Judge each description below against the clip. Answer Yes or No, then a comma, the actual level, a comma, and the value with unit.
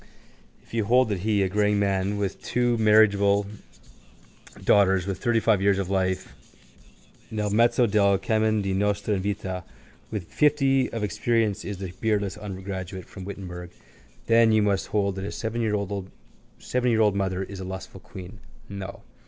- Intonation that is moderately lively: No, narrow, 2.2 semitones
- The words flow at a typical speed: Yes, average, 150 wpm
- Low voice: Yes, low, 100 Hz